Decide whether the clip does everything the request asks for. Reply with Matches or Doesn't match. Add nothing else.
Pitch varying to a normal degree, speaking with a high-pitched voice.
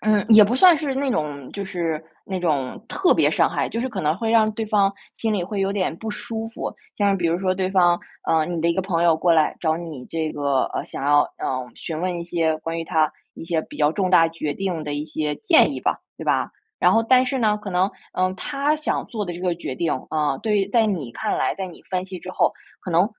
Doesn't match